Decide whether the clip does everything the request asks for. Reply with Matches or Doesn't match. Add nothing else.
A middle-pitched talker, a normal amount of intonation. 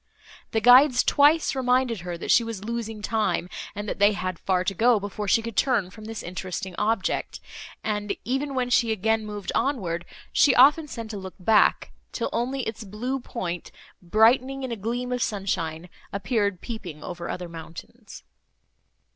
Doesn't match